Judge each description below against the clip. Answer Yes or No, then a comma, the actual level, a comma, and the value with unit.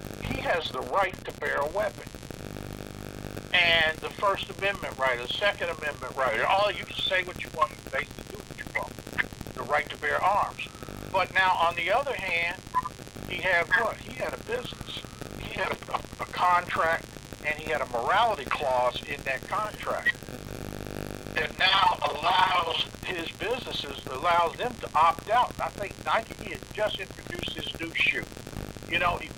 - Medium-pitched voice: Yes, medium, 155 Hz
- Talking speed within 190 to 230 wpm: No, average, 170 wpm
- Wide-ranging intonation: Yes, wide, 6.1 semitones